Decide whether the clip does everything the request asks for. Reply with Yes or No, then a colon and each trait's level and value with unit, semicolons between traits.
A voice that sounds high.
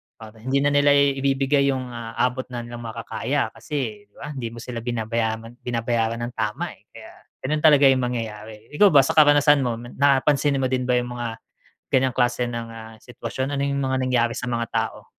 No: low, 125 Hz